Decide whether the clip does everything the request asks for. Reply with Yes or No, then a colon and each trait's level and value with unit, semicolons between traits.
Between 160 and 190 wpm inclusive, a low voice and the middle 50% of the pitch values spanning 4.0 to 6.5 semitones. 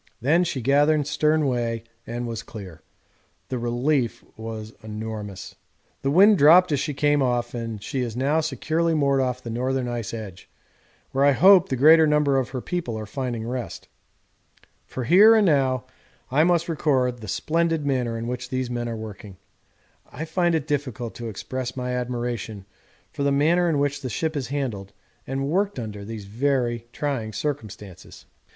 Yes: average, 170 wpm; low, 130 Hz; average, 4.3 semitones